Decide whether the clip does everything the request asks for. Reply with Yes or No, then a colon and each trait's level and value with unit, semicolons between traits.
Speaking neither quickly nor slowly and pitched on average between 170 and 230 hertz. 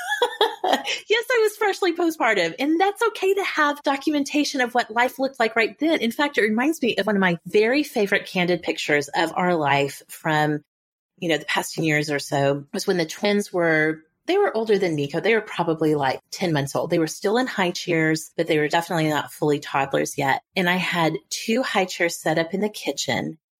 No: fast, 215 wpm; high, 190 Hz